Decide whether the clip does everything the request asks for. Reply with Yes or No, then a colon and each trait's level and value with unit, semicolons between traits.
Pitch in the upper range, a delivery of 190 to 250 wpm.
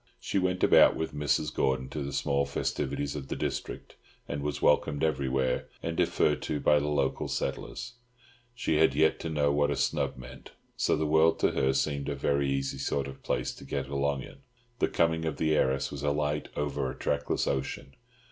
No: very low, 70 Hz; average, 200 wpm